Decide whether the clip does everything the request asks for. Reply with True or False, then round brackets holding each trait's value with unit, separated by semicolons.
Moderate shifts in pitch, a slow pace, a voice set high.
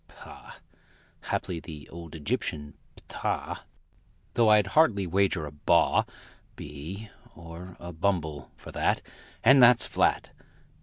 False (4.6 semitones; 115 wpm; 85 Hz)